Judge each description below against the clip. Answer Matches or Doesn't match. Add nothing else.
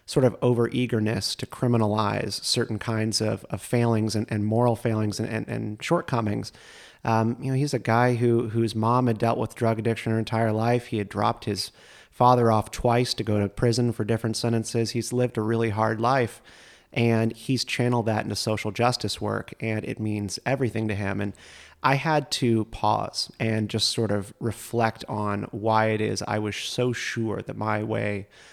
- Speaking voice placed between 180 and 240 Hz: Doesn't match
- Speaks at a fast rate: Doesn't match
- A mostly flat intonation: Matches